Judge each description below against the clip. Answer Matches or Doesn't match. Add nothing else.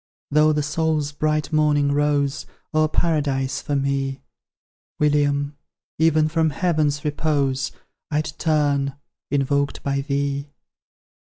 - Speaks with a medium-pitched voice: Matches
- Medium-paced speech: Doesn't match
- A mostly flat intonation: Matches